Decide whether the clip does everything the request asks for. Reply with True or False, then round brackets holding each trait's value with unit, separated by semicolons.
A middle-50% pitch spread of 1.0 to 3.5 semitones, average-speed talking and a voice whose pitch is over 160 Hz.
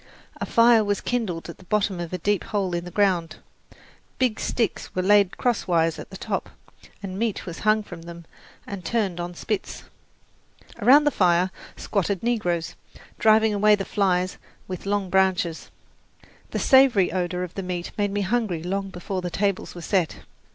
True (3.0 semitones; 170 wpm; 190 Hz)